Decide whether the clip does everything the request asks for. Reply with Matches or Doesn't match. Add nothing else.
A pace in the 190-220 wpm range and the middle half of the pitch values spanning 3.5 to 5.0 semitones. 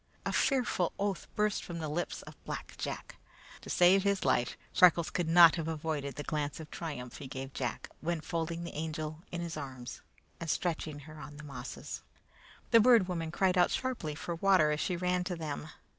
Doesn't match